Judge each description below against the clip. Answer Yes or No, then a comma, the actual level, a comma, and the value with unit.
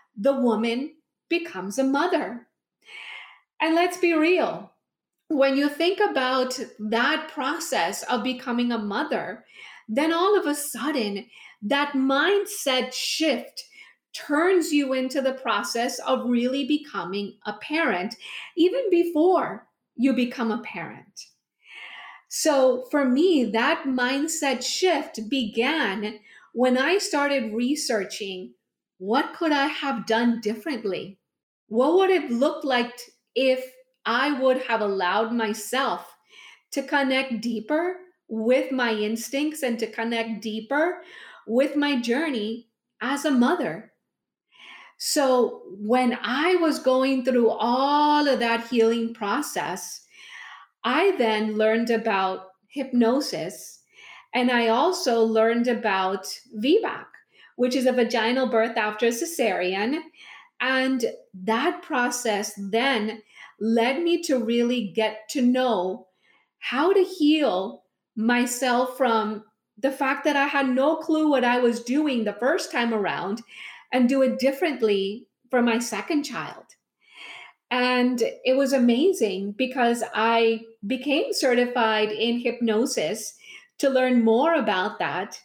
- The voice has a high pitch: Yes, very high, 255 Hz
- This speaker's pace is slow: Yes, slow, 120 wpm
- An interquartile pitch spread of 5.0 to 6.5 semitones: No, average, 4.2 semitones